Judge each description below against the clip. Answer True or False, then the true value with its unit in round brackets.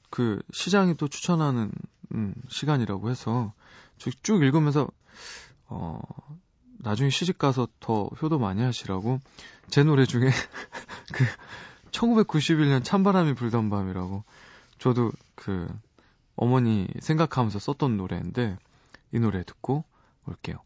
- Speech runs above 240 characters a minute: False (235 characters per minute)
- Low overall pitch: True (130 Hz)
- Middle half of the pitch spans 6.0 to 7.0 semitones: False (5.2 semitones)